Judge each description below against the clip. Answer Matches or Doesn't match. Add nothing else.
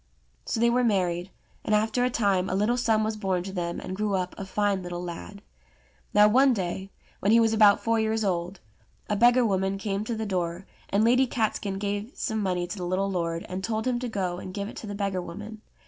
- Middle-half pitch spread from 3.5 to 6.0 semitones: Doesn't match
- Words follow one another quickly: Matches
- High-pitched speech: Matches